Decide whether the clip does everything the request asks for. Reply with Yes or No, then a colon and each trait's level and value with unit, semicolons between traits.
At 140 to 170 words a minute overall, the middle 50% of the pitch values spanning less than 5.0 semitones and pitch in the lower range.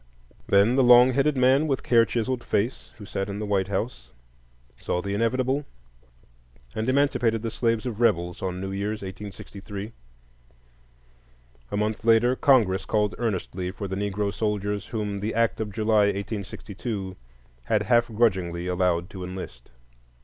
Yes: average, 150 wpm; average, 3.2 semitones; low, 105 Hz